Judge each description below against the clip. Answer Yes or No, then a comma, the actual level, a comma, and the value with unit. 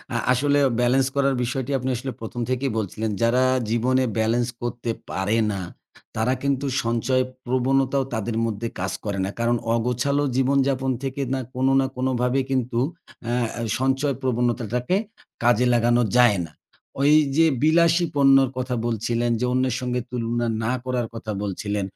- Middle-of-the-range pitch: No, low, 125 Hz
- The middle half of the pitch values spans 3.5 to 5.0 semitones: No, narrow, 2.4 semitones